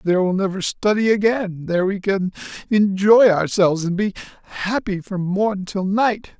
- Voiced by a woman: No, male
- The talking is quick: No, average, 160 wpm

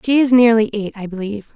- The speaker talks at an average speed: No, fast, 230 wpm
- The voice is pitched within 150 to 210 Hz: No, high, 220 Hz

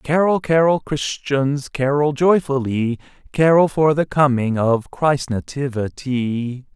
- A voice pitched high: No, medium, 140 Hz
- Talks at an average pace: No, slow, 105 wpm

